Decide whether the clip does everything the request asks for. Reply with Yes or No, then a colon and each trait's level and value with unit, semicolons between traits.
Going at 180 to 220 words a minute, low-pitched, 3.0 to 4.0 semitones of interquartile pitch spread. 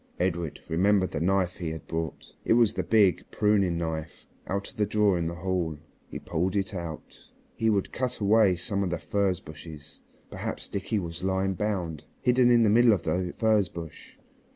Yes: average, 190 wpm; very low, 95 Hz; average, 3.6 semitones